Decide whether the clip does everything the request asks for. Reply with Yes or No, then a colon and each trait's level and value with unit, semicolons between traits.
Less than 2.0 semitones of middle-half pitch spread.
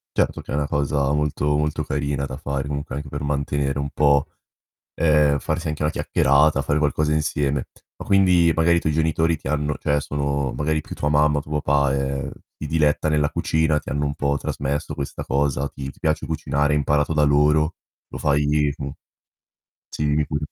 Yes: narrow, 1.2 semitones